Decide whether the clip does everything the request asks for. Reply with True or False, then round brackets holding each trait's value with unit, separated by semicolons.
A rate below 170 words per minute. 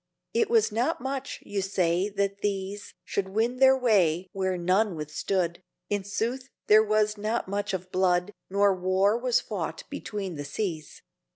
True (160 wpm)